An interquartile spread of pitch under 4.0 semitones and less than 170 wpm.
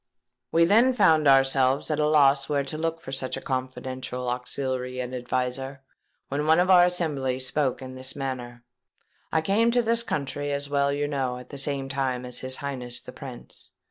No: average, 2.8 semitones; average, 185 wpm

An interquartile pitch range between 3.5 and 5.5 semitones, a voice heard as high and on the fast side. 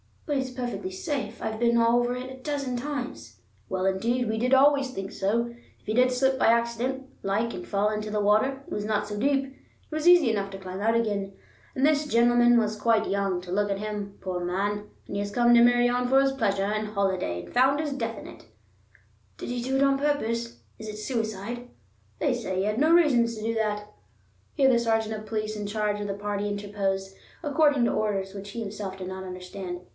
Yes: average, 3.8 semitones; high, 225 Hz; fast, 220 wpm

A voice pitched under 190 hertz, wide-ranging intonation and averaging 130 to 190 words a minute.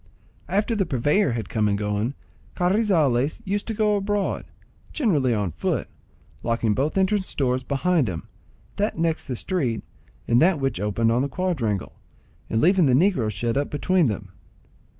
Yes: medium, 140 Hz; wide, 8.4 semitones; average, 150 wpm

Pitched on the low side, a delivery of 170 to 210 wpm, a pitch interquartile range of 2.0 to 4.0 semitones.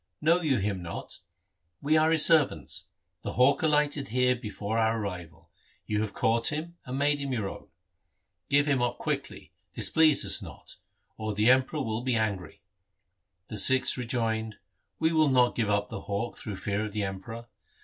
No: low, 120 Hz; average, 175 wpm; average, 5.2 semitones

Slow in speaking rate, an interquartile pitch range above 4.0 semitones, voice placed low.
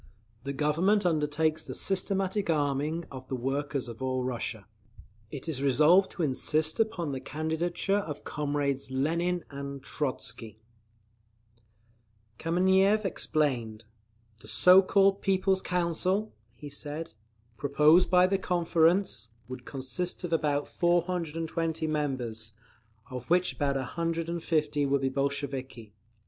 No: slow, 115 wpm; average, 4.4 semitones; medium, 155 Hz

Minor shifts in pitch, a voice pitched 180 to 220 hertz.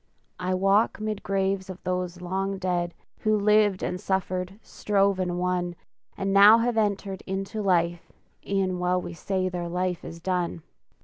Yes: narrow, 1.6 semitones; medium, 185 Hz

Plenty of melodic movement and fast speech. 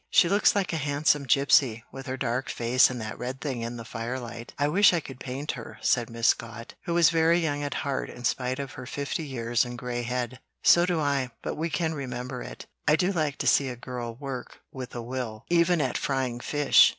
No: average, 3.5 semitones; fast, 225 wpm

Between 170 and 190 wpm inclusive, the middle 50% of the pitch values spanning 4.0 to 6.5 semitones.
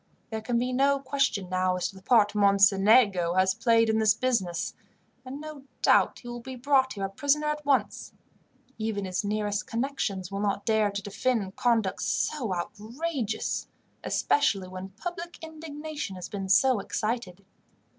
No: average, 160 wpm; average, 5.0 semitones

